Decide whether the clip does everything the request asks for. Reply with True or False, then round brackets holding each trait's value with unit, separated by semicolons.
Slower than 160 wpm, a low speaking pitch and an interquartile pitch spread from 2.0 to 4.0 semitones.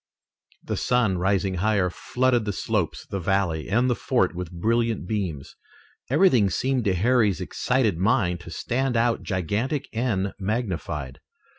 False (140 wpm; 105 Hz; 4.9 semitones)